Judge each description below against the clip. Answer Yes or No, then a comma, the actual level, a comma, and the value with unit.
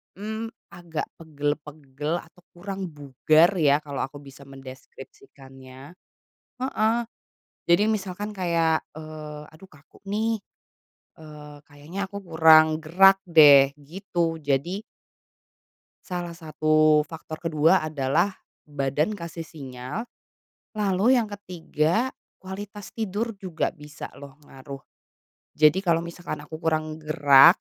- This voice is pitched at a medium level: Yes, medium, 160 Hz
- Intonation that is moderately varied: Yes, average, 4.3 semitones